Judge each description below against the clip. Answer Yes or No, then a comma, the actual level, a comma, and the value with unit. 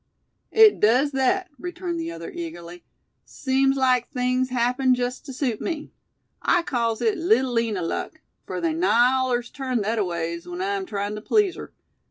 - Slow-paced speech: No, average, 165 wpm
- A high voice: Yes, very high, 255 Hz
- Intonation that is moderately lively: No, wide, 6.0 semitones